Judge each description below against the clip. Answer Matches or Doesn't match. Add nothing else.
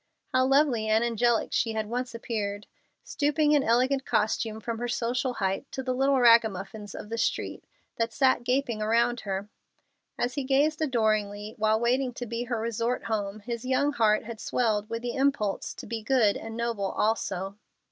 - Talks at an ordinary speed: Matches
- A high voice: Matches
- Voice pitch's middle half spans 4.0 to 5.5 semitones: Doesn't match